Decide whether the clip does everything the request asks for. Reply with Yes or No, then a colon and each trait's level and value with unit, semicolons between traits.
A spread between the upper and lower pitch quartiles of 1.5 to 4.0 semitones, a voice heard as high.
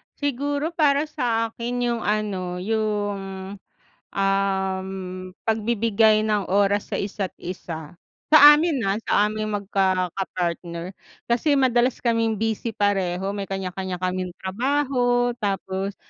Yes: average, 3.7 semitones; high, 205 Hz